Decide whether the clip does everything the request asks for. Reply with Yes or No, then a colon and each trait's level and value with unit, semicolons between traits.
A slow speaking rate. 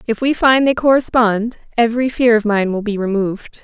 No: average, 200 wpm